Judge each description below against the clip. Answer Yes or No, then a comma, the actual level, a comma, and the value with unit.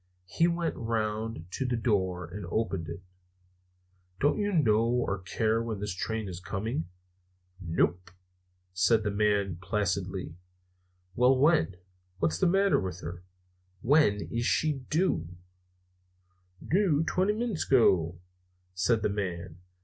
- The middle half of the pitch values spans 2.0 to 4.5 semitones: No, wide, 5.6 semitones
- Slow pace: Yes, slow, 125 wpm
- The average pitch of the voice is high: No, low, 105 Hz